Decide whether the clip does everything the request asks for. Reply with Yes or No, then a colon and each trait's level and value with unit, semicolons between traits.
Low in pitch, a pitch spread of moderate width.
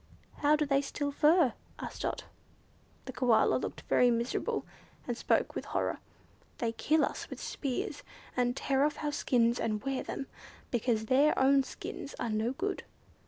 No: very high, 265 Hz; average, 3.3 semitones